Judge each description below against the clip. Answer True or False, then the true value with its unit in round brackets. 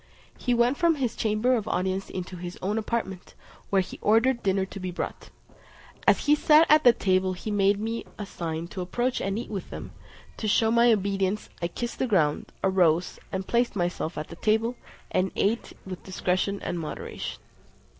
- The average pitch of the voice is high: True (200 Hz)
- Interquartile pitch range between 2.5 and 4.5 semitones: True (4.1 semitones)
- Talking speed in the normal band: True (185 wpm)